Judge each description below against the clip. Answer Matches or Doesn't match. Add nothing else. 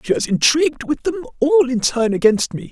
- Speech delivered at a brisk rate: Matches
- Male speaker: Matches